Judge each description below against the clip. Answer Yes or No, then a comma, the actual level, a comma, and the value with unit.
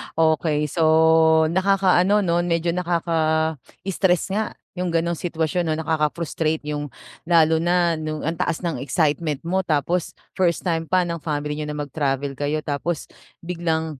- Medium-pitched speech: Yes, medium, 165 Hz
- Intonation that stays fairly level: Yes, narrow, 2.3 semitones